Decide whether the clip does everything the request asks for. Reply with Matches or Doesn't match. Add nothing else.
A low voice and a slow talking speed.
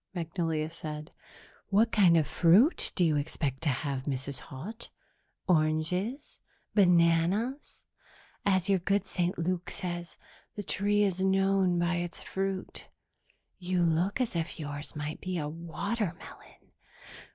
Doesn't match